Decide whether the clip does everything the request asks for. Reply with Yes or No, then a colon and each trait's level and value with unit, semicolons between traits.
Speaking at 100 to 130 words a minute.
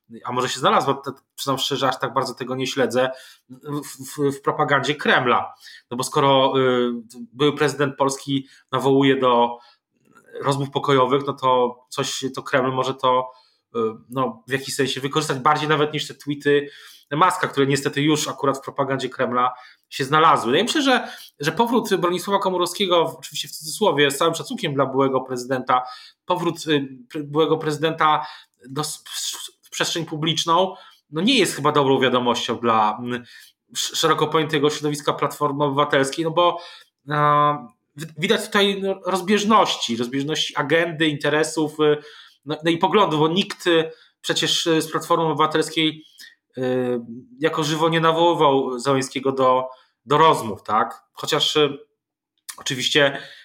No: average, 140 wpm